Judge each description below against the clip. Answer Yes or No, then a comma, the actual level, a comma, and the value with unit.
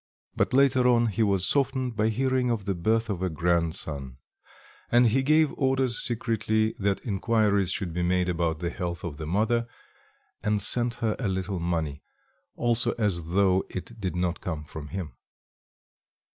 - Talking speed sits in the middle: Yes, average, 165 wpm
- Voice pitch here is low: Yes, low, 100 Hz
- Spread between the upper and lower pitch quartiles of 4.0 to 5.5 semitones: Yes, average, 5.2 semitones